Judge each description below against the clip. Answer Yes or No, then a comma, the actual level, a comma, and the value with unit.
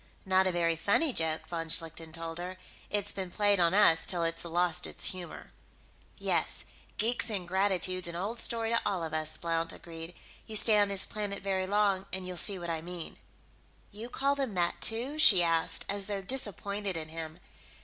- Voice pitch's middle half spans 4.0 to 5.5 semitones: No, average, 3.6 semitones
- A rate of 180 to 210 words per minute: Yes, average, 190 wpm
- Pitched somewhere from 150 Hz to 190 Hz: Yes, medium, 185 Hz